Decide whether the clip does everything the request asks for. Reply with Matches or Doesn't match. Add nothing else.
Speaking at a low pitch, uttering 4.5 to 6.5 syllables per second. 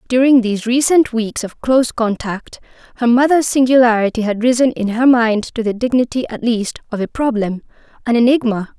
Doesn't match